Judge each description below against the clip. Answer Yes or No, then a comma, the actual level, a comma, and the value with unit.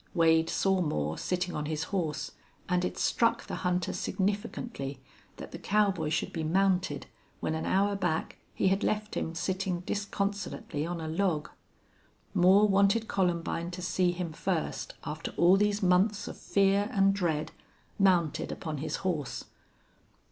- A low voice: No, medium, 180 Hz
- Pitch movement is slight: No, average, 3.4 semitones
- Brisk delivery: No, average, 150 wpm